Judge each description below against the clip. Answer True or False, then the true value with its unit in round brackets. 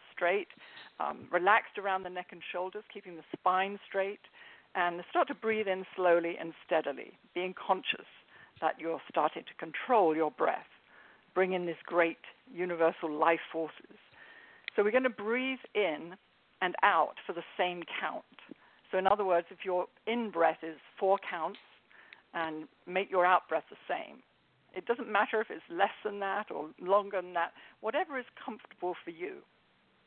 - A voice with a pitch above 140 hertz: True (185 Hz)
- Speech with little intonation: False (3.8 semitones)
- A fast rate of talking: False (165 wpm)